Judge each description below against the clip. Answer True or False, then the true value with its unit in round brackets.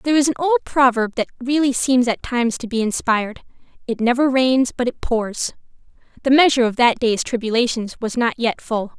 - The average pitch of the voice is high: True (245 Hz)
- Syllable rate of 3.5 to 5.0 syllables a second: False (5.6 syllables/s)